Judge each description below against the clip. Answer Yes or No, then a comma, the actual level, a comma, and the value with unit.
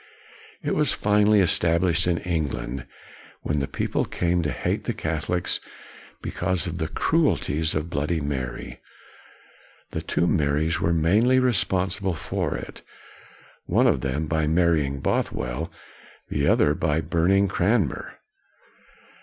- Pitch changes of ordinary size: Yes, average, 3.6 semitones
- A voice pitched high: No, very low, 85 Hz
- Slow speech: Yes, slow, 125 wpm